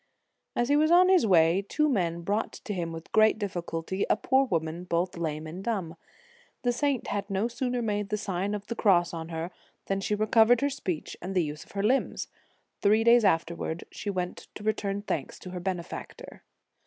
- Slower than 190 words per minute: No, fast, 205 wpm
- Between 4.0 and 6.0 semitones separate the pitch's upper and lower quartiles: Yes, average, 4.7 semitones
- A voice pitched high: Yes, high, 195 Hz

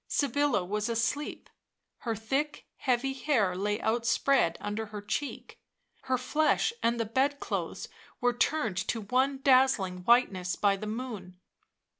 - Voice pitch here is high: Yes, high, 235 Hz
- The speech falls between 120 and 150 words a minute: Yes, slow, 135 wpm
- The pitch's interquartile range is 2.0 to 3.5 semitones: No, average, 4.5 semitones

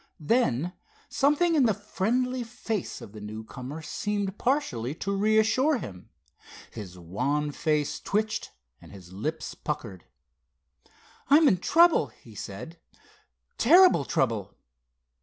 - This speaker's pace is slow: Yes, slow, 110 wpm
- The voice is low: No, medium, 165 Hz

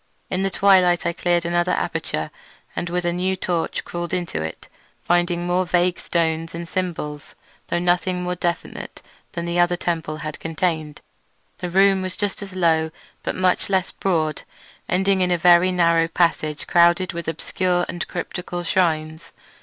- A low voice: No, medium, 175 Hz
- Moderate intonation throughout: No, narrow, 1.5 semitones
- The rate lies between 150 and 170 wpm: Yes, average, 160 wpm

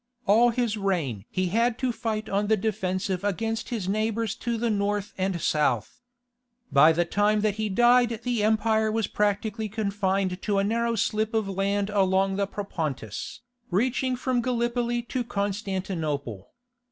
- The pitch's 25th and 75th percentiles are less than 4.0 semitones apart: Yes, average, 2.9 semitones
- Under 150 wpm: No, average, 155 wpm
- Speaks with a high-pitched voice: Yes, high, 210 Hz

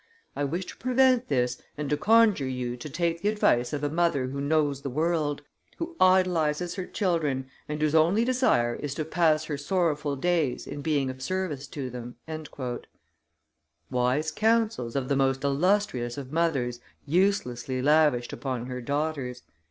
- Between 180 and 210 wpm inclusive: No, average, 160 wpm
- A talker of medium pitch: Yes, medium, 150 Hz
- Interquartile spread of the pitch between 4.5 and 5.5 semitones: Yes, average, 5.0 semitones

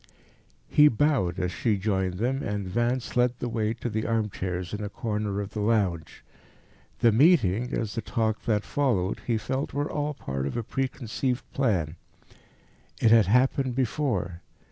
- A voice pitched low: Yes, low, 110 Hz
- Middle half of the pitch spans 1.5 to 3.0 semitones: No, average, 4.3 semitones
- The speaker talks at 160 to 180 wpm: Yes, average, 165 wpm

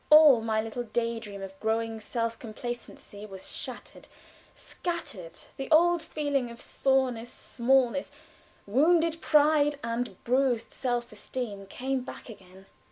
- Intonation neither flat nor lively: Yes, average, 3.8 semitones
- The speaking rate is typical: No, slow, 125 wpm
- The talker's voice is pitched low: No, high, 240 Hz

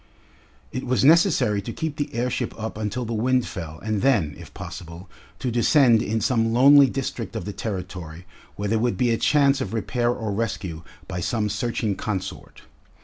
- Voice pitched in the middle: No, low, 115 Hz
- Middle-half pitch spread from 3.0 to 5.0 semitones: Yes, average, 4.1 semitones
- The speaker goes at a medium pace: Yes, average, 180 wpm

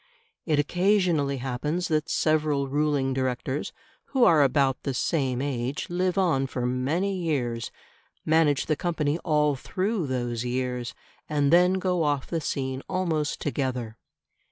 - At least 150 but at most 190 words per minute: No, slow, 135 wpm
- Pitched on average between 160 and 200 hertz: No, medium, 145 Hz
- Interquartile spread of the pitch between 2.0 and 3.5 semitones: No, average, 4.2 semitones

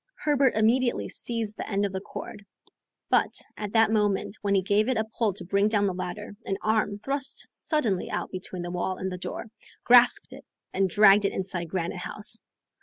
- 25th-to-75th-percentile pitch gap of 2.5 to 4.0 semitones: Yes, average, 2.8 semitones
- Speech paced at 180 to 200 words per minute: Yes, average, 195 wpm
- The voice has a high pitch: Yes, high, 205 Hz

